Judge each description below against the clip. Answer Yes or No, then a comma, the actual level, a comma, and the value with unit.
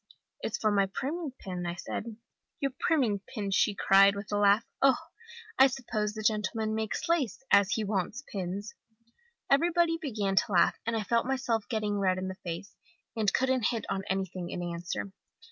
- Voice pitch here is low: No, high, 210 Hz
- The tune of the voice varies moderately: Yes, average, 3.8 semitones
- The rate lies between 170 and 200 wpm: Yes, average, 180 wpm